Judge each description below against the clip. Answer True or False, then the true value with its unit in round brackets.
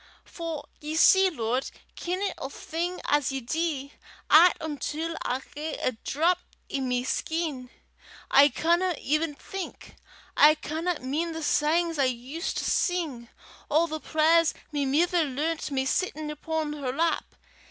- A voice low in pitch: False (310 Hz)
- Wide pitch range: False (3.2 semitones)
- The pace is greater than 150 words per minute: False (145 wpm)